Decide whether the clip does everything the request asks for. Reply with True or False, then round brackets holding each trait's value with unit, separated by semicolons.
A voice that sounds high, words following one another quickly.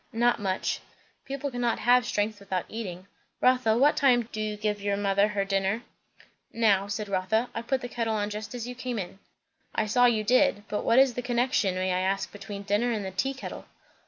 True (215 Hz; 210 wpm)